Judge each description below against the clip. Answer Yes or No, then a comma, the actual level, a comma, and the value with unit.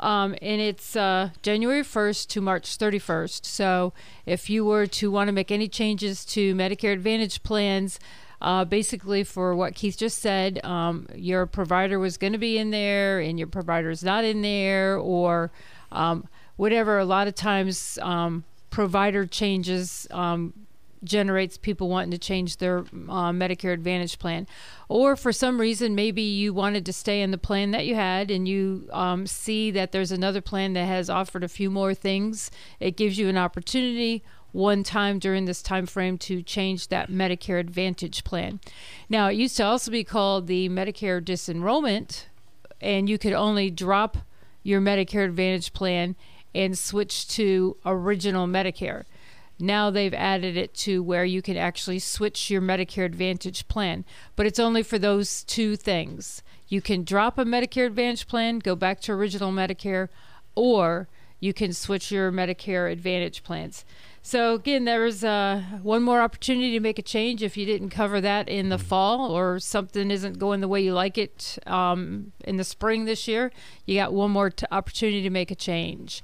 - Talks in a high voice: Yes, high, 195 Hz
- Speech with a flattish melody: Yes, narrow, 2.2 semitones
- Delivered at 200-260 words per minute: No, average, 175 wpm